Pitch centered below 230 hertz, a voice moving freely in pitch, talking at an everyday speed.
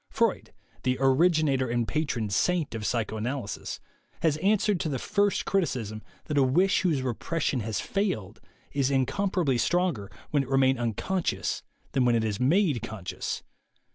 Yes: low, 135 Hz; wide, 6.5 semitones; average, 150 wpm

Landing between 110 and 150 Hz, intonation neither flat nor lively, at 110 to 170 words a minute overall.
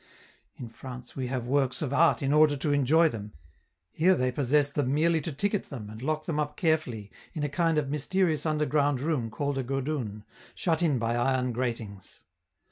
No: medium, 140 Hz; average, 3.7 semitones; average, 190 wpm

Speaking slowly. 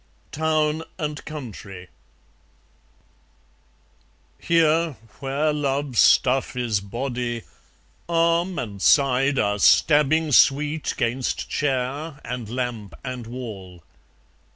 Yes: slow, 85 wpm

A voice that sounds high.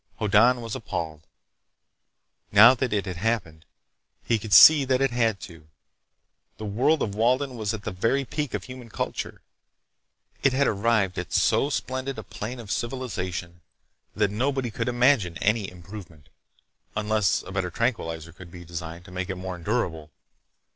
No: low, 105 Hz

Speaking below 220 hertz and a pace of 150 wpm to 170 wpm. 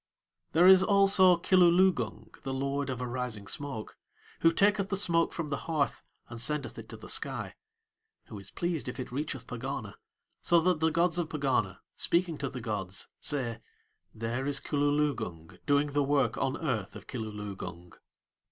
Yes: medium, 140 Hz; average, 160 wpm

